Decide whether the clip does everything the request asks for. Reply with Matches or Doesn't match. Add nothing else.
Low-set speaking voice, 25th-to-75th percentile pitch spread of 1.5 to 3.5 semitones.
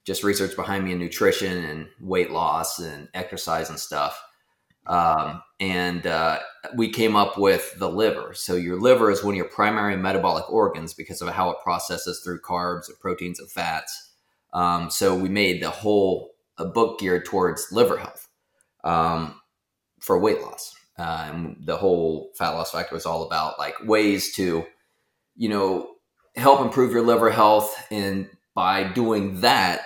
Matches